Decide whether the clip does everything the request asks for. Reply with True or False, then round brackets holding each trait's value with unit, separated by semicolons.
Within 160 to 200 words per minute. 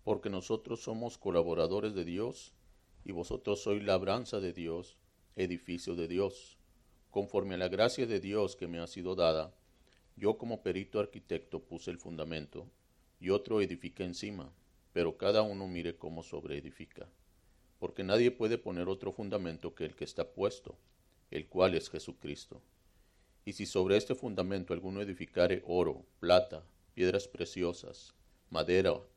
False (145 wpm)